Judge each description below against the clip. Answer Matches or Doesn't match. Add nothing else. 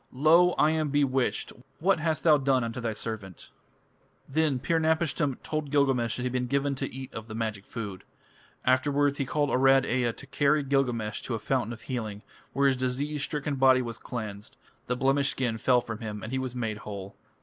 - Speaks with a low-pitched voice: Matches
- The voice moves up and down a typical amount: Matches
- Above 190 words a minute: Matches